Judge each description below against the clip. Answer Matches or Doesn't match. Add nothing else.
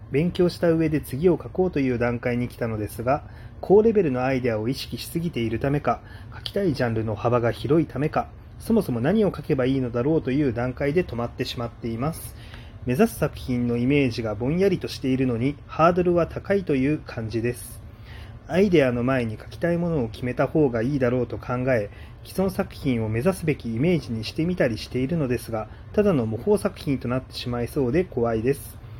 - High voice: Doesn't match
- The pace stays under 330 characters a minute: Doesn't match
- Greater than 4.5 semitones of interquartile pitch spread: Matches